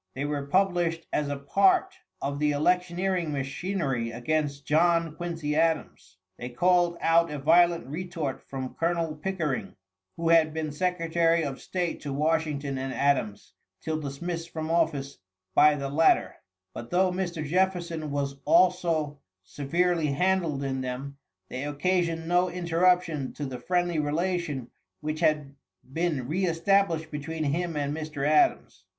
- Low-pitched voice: No, medium, 160 Hz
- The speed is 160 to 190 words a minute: No, average, 140 wpm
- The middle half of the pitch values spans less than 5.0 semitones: Yes, average, 3.5 semitones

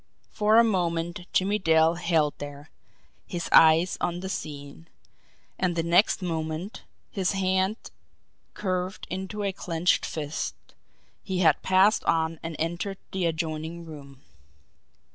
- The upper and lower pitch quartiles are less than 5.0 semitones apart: Yes, average, 2.8 semitones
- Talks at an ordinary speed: No, slow, 125 wpm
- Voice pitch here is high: No, medium, 170 Hz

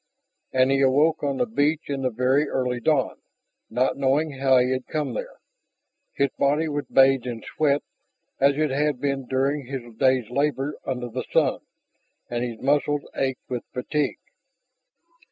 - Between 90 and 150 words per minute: No, average, 160 wpm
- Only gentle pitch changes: Yes, narrow, 2.2 semitones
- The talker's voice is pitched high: No, low, 135 Hz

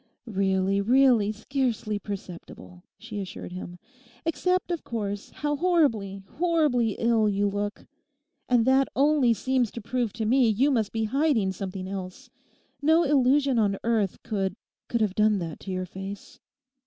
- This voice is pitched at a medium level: No, high, 220 Hz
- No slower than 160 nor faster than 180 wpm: No, average, 145 wpm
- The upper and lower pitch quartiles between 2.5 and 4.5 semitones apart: No, average, 5.1 semitones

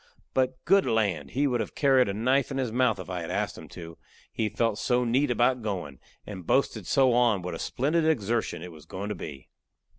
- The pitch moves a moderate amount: No, wide, 5.7 semitones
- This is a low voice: Yes, low, 115 Hz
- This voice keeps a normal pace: No, fast, 220 wpm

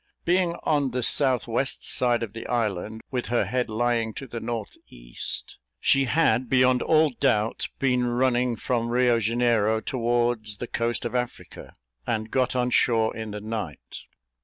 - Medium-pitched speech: No, low, 120 Hz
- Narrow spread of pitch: Yes, narrow, 2.2 semitones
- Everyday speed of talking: Yes, average, 160 wpm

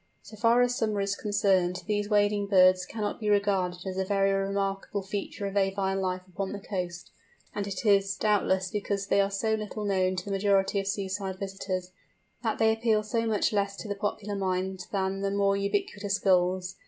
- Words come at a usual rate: Yes, average, 190 wpm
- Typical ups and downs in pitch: No, narrow, 1.4 semitones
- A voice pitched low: No, high, 200 Hz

